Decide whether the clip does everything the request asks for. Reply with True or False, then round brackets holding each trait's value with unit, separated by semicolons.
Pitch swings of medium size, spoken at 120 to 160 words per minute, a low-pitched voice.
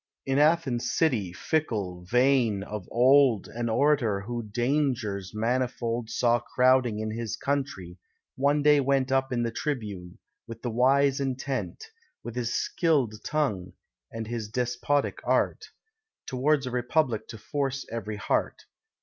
True (3.8 semitones; 135 wpm; 125 Hz)